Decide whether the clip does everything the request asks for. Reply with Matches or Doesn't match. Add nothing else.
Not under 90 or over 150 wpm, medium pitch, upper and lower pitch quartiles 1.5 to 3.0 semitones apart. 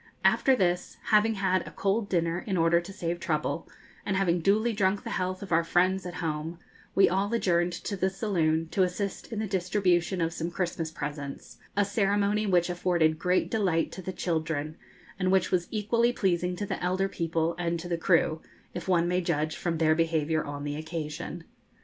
Doesn't match